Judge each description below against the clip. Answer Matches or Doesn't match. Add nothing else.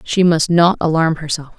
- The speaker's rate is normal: Matches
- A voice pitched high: Doesn't match